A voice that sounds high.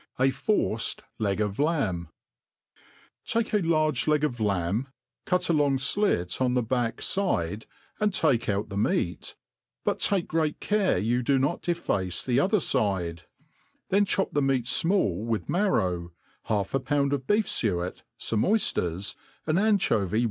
No: low, 130 Hz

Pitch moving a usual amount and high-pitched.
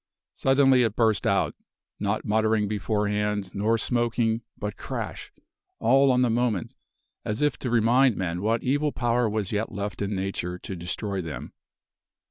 No: average, 3.0 semitones; low, 110 Hz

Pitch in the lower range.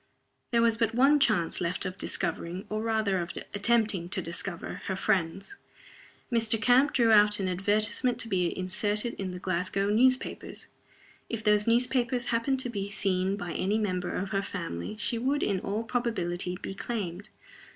No: high, 205 Hz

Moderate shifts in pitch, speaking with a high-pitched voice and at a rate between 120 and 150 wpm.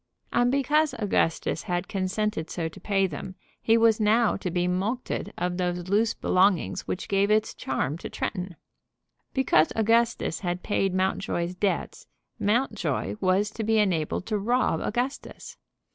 Yes: average, 3.8 semitones; high, 195 Hz; average, 145 wpm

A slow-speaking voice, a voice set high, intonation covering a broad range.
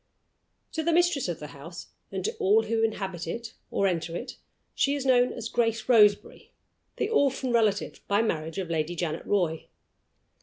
No: average, 175 wpm; high, 220 Hz; wide, 6.9 semitones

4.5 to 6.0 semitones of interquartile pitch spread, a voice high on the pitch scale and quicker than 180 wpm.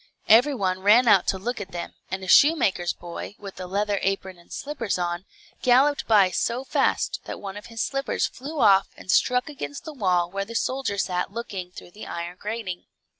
Yes: average, 4.8 semitones; high, 200 Hz; average, 200 wpm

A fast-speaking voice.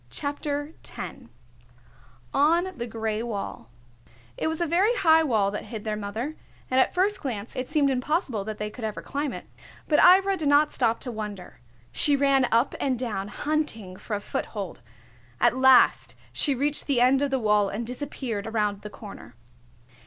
No: average, 175 wpm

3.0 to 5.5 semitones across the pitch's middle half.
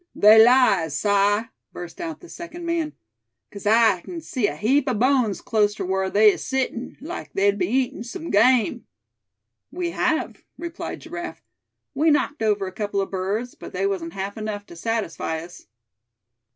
Yes: average, 5.2 semitones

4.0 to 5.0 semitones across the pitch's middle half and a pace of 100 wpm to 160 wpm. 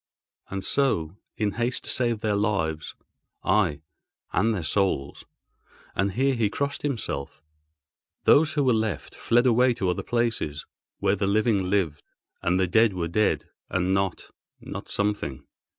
Yes: average, 4.4 semitones; average, 140 wpm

